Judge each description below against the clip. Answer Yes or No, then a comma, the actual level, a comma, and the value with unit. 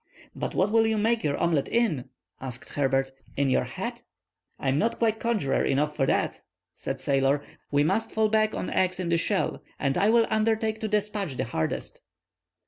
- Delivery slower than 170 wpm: No, average, 195 wpm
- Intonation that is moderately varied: No, wide, 8.0 semitones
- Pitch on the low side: No, medium, 185 Hz